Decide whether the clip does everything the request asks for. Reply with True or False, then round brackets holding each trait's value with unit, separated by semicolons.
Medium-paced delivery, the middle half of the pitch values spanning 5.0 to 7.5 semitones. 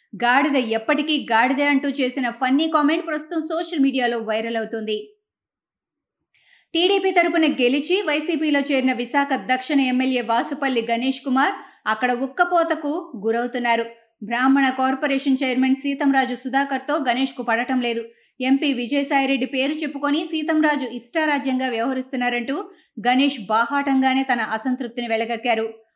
False (110 wpm; 3.2 semitones)